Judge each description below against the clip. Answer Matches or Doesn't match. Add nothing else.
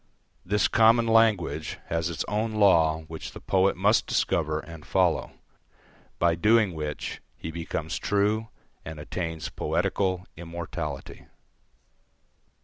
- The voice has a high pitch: Doesn't match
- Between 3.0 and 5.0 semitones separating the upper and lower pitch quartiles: Matches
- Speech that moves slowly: Matches